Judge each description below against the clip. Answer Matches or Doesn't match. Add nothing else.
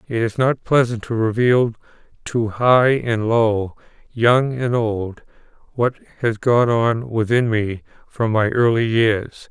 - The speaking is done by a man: Matches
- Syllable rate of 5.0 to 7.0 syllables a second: Doesn't match